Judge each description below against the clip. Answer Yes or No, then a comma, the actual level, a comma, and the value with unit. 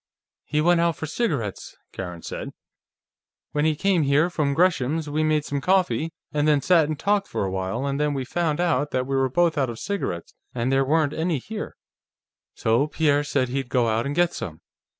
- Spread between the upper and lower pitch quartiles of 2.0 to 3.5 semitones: No, average, 3.9 semitones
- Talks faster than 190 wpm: Yes, fast, 205 wpm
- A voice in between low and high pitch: Yes, medium, 145 Hz